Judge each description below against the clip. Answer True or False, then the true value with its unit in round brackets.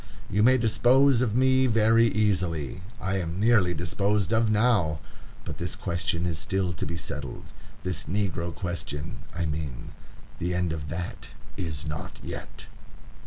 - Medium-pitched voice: False (90 Hz)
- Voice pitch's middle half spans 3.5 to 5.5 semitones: True (4.7 semitones)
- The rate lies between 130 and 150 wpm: True (145 wpm)